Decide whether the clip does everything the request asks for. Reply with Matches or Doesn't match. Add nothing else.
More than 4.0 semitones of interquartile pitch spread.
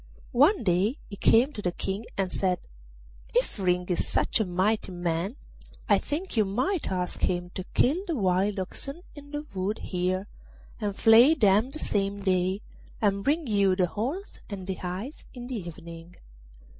Matches